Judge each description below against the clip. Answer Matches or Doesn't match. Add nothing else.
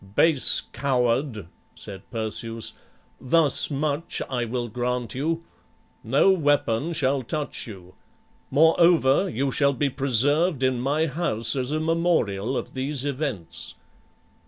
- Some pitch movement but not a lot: Matches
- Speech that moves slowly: Matches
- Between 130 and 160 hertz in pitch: Matches